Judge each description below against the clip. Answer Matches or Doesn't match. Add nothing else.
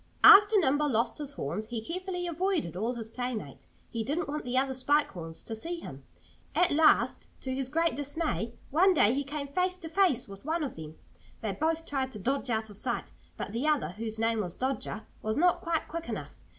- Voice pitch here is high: Matches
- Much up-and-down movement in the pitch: Matches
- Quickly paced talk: Matches